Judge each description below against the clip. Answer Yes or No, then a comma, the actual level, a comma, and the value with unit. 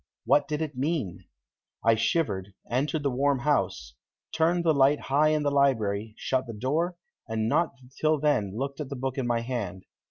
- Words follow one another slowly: No, average, 185 wpm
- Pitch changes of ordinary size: Yes, average, 4.6 semitones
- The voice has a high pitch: No, low, 135 Hz